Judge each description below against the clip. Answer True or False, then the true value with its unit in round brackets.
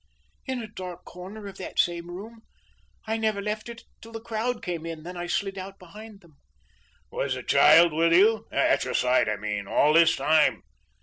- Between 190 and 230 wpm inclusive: True (195 wpm)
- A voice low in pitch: False (185 Hz)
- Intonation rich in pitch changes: False (4.7 semitones)